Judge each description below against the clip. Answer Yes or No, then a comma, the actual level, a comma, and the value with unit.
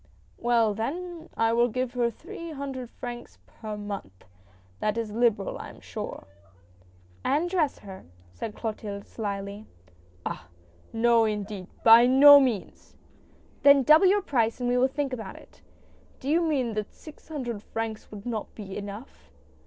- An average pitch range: Yes, average, 4.5 semitones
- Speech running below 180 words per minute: Yes, average, 160 wpm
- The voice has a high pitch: Yes, high, 235 Hz